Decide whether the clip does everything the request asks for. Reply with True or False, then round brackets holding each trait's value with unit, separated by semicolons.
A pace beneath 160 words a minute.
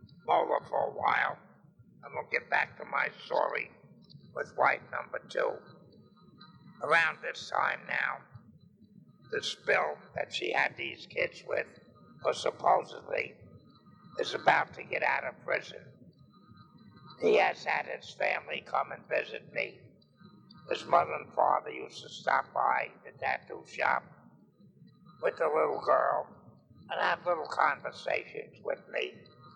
True (135 wpm)